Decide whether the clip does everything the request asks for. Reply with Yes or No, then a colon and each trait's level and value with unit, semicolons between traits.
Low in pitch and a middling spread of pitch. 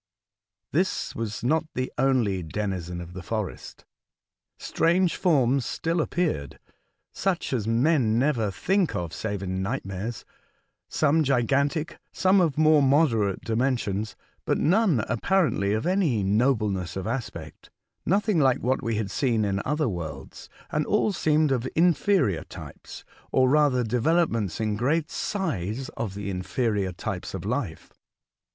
No: low, 125 Hz; wide, 7.2 semitones